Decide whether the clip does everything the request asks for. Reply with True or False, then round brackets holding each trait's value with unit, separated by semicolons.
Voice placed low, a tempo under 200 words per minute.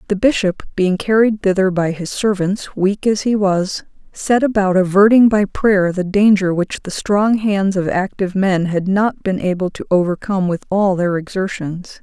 False (195 Hz; 180 wpm)